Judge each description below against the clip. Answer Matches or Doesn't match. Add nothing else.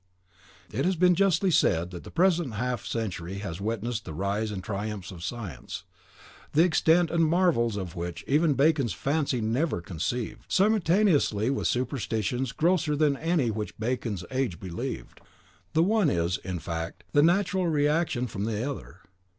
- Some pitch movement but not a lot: Doesn't match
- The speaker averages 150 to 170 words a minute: Matches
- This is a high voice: Doesn't match